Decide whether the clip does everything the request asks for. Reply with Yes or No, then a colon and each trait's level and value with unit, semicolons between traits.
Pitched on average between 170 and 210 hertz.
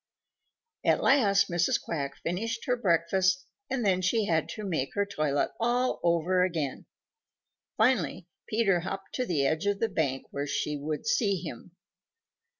Yes: medium, 185 Hz